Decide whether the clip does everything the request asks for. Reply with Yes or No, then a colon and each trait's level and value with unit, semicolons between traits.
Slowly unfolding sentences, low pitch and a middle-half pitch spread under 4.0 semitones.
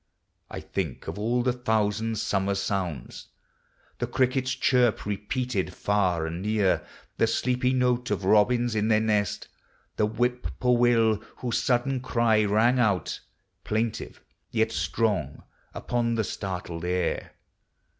Yes: slow, 125 wpm; low, 110 Hz; average, 3.5 semitones